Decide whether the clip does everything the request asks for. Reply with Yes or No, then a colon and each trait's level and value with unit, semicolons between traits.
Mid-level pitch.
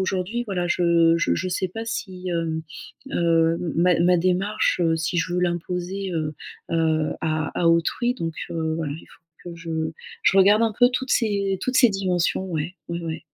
Yes: medium, 175 Hz